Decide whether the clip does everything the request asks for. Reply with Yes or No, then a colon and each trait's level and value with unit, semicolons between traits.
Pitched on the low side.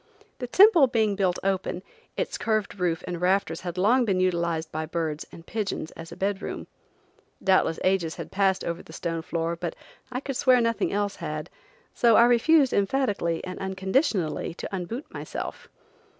No: high, 190 Hz